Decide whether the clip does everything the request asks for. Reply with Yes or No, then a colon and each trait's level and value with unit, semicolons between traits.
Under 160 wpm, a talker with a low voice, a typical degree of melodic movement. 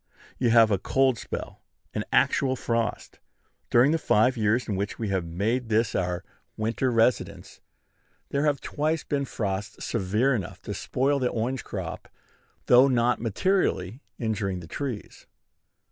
Yes: average, 145 wpm; low, 115 Hz; average, 4.0 semitones